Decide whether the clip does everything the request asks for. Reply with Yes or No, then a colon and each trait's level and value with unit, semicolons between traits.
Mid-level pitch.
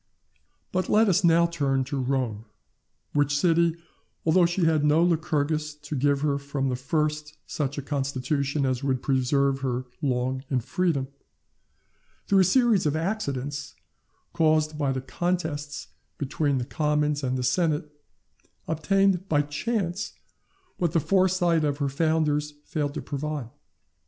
Yes: medium, 150 Hz